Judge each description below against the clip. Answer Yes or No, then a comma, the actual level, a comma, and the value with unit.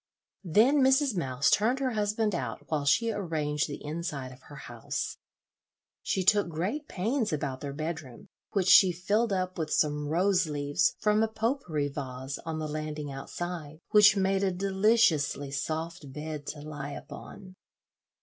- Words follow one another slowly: No, average, 160 wpm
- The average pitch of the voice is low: No, medium, 165 Hz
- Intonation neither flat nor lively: No, wide, 5.7 semitones